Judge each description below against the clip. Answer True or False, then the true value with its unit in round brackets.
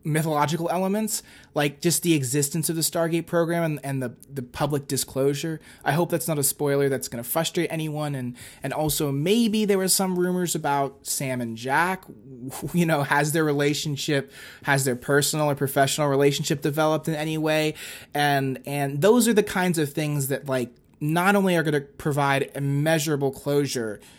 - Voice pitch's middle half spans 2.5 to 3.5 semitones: True (2.9 semitones)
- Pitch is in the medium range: True (150 Hz)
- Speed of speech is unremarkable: True (175 wpm)